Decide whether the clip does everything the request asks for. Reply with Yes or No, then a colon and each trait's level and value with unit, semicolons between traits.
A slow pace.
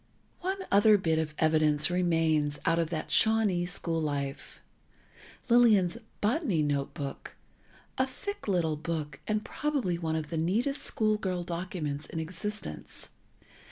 Yes: slow, 125 wpm